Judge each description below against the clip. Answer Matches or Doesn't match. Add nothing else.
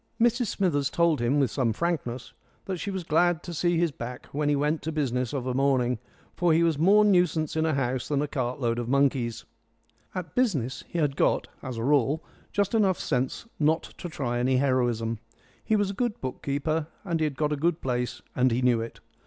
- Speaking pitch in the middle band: Matches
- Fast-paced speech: Matches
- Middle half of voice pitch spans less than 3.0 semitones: Doesn't match